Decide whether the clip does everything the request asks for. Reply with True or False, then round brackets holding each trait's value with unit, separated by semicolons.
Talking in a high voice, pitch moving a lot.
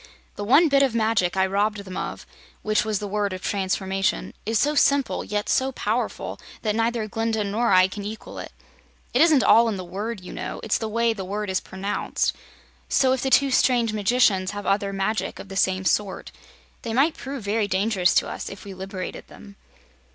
False (210 Hz; 3.1 semitones)